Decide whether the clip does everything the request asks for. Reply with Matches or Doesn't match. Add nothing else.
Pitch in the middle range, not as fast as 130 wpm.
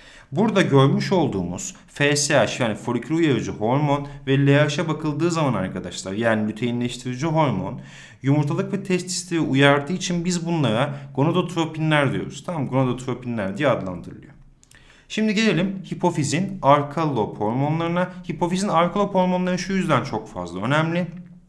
Matches